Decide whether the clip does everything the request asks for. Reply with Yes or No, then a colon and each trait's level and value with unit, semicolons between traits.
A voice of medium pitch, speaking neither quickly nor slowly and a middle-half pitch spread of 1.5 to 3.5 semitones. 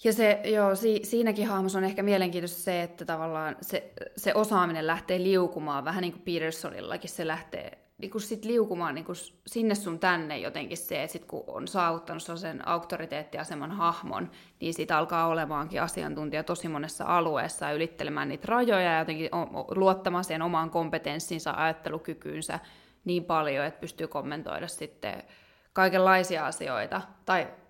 Yes: medium, 170 Hz; average, 145 wpm; average, 2.9 semitones